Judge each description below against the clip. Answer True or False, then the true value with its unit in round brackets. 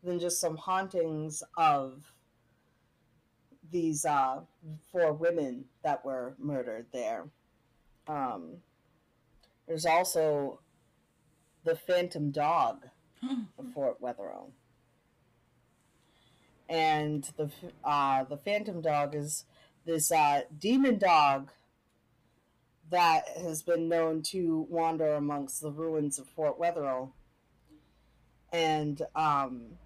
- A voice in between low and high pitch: True (155 Hz)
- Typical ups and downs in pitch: True (3.4 semitones)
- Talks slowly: True (95 wpm)